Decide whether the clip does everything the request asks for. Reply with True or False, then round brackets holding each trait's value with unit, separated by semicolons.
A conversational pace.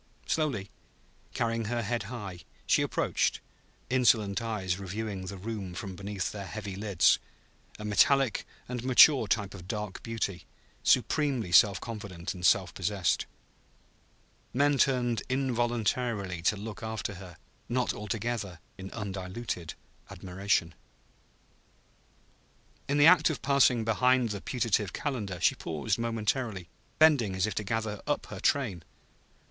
False (130 wpm)